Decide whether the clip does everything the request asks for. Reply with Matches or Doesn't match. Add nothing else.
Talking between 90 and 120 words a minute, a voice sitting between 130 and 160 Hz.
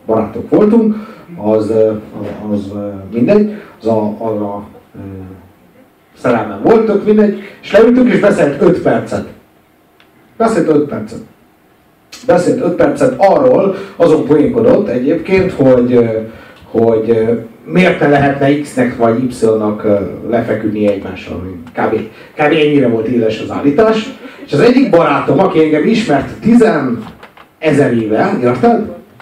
Matches